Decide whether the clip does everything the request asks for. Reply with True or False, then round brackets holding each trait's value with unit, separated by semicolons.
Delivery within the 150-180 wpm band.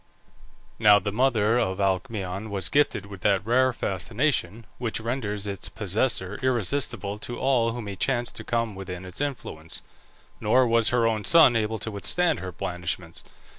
True (160 wpm)